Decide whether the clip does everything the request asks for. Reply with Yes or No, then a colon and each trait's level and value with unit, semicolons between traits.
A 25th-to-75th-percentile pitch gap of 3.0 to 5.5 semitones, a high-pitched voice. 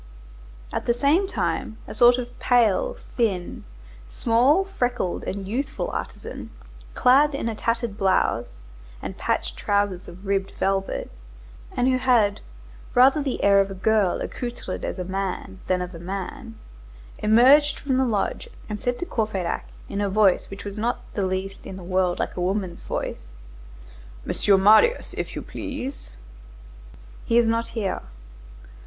Yes: average, 4.3 semitones; high, 215 Hz